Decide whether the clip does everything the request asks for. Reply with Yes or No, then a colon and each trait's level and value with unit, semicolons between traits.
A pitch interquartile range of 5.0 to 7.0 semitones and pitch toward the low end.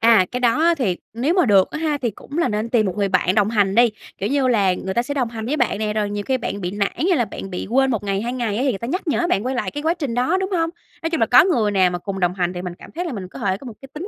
No: wide, 5.6 semitones; high, 230 Hz